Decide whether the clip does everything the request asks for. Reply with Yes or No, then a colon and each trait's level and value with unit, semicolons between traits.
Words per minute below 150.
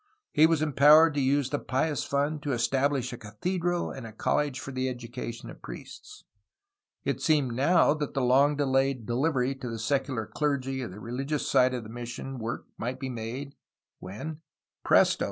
No: average, 175 wpm